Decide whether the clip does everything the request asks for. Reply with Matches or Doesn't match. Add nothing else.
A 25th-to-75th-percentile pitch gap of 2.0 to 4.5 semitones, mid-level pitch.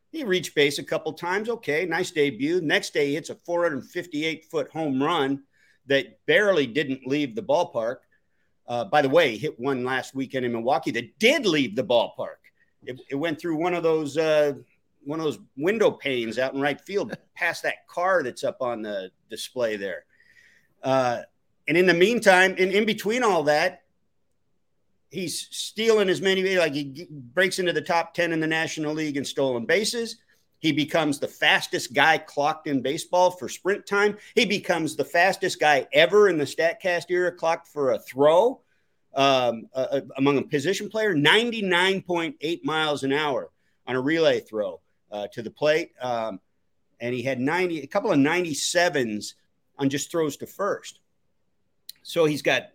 Doesn't match